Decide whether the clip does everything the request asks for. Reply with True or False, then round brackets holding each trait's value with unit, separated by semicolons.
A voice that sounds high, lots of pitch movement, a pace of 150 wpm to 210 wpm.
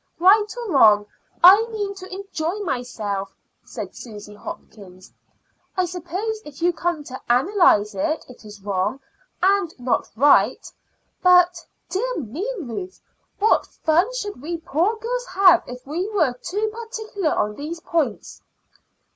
False (340 Hz; 8.2 semitones; 140 wpm)